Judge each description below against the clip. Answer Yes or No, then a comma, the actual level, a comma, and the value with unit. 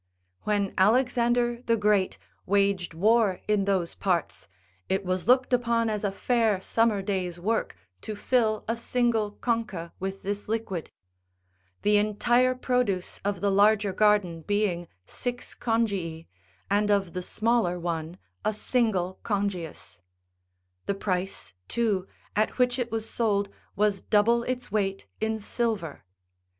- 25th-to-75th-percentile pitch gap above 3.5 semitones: No, average, 3.2 semitones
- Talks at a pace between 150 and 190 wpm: No, slow, 135 wpm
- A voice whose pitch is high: Yes, high, 205 Hz